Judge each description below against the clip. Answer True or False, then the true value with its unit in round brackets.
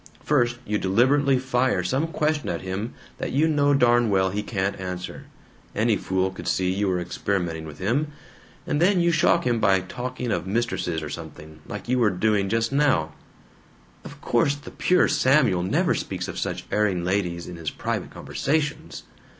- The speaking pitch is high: False (105 Hz)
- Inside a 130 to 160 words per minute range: False (180 wpm)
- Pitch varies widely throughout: True (6.3 semitones)